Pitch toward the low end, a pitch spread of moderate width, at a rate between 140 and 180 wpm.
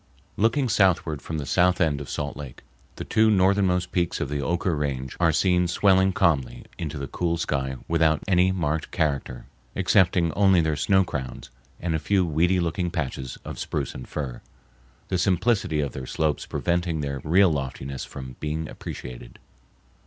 Yes: very low, 80 Hz; average, 4.2 semitones; average, 165 wpm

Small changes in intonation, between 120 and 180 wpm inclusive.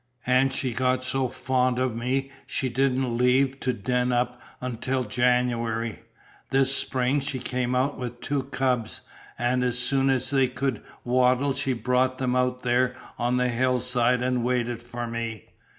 Yes: narrow, 1.1 semitones; average, 160 wpm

